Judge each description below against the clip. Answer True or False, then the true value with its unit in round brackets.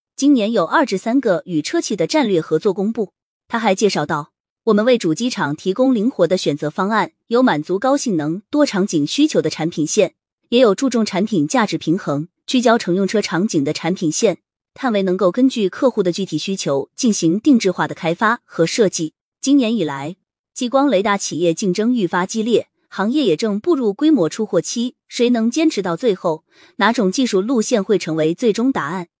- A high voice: True (205 Hz)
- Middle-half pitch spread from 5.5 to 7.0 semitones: True (6.6 semitones)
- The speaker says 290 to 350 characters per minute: True (295 characters per minute)